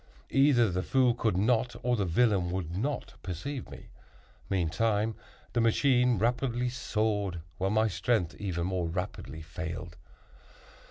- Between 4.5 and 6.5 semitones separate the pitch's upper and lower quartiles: Yes, average, 5.2 semitones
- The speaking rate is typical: No, slow, 130 wpm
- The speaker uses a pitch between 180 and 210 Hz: No, low, 105 Hz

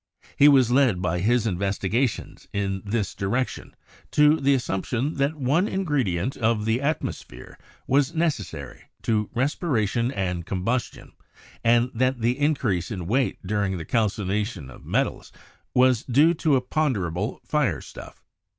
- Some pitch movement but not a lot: No, wide, 5.7 semitones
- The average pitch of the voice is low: Yes, low, 120 Hz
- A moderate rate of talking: No, slow, 130 wpm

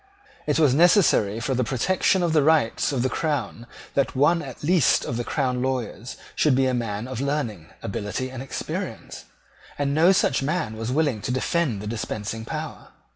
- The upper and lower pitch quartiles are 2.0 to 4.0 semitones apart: No, average, 4.7 semitones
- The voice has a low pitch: Yes, low, 130 Hz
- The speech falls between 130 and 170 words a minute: No, average, 180 wpm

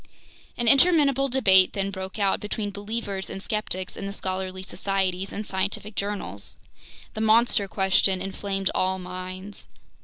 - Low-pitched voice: No, high, 195 Hz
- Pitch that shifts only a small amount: Yes, narrow, 2.0 semitones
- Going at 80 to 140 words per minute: Yes, slow, 135 wpm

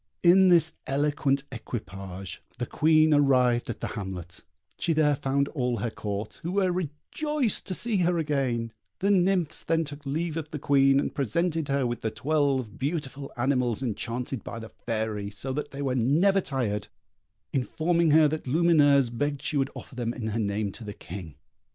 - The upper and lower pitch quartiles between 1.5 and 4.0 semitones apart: No, average, 5.0 semitones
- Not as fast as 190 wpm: Yes, average, 175 wpm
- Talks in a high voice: No, medium, 140 Hz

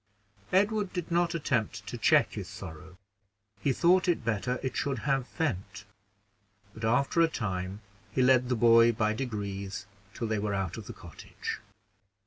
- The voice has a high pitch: No, low, 115 Hz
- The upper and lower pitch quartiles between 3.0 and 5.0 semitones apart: No, wide, 5.6 semitones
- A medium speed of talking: Yes, average, 160 wpm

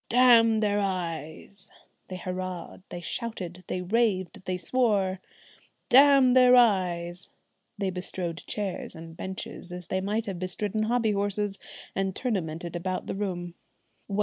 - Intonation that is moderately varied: Yes, average, 3.3 semitones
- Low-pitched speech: No, high, 190 Hz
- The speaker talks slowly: Yes, slow, 130 wpm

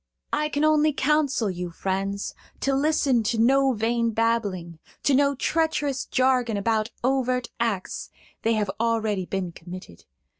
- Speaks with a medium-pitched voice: No, high, 230 Hz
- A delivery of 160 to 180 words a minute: No, average, 140 wpm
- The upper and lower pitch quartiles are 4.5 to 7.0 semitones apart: Yes, average, 5.3 semitones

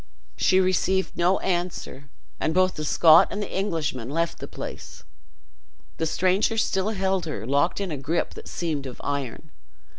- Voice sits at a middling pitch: Yes, medium, 170 Hz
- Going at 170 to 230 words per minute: No, average, 160 wpm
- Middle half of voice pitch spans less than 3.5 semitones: No, average, 4.0 semitones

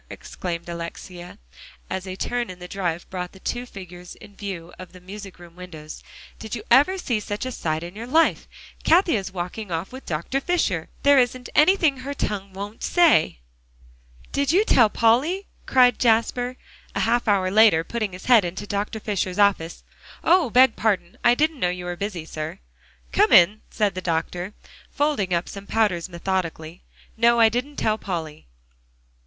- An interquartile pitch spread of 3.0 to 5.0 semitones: No, wide, 5.5 semitones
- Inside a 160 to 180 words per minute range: Yes, average, 175 wpm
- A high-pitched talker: Yes, high, 200 Hz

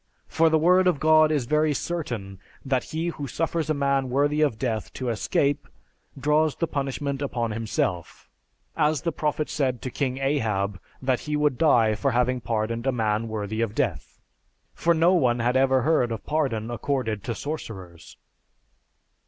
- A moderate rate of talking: Yes, average, 170 wpm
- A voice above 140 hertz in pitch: No, low, 135 Hz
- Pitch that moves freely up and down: No, average, 4.8 semitones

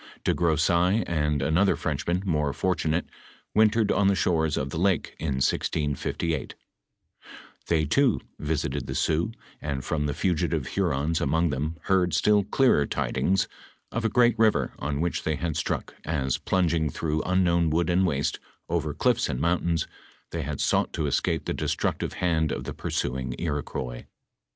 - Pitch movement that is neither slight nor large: Yes, average, 3.5 semitones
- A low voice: Yes, very low, 80 Hz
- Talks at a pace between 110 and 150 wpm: No, average, 165 wpm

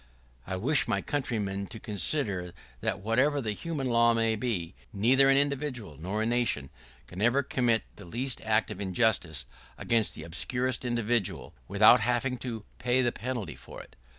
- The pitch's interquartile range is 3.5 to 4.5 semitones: Yes, average, 4.2 semitones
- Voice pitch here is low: Yes, low, 115 Hz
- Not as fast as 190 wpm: Yes, average, 170 wpm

